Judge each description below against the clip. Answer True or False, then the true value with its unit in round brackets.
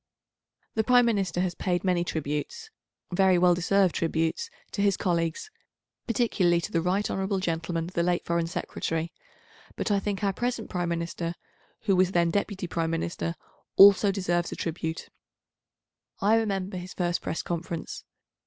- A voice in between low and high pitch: True (180 Hz)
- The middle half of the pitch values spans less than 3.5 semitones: True (2.8 semitones)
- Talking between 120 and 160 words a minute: True (155 wpm)